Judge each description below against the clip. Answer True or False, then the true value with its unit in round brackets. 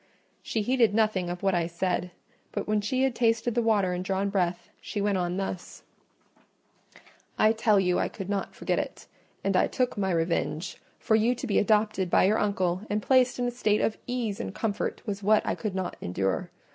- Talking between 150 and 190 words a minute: False (205 wpm)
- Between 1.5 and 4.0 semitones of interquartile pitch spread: True (3.3 semitones)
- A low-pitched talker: False (205 Hz)